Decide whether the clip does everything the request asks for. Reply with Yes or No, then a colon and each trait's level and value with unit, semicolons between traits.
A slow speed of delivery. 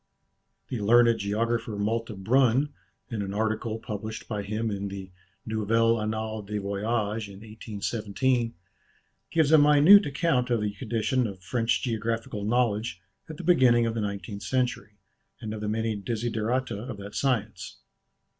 No: average, 145 wpm